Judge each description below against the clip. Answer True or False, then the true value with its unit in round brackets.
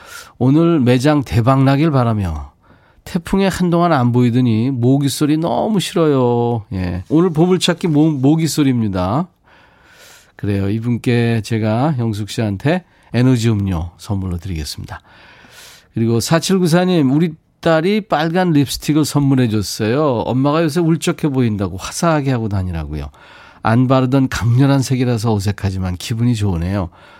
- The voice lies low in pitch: True (125 Hz)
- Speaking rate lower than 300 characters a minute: False (305 characters per minute)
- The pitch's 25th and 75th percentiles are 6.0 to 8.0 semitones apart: True (6.8 semitones)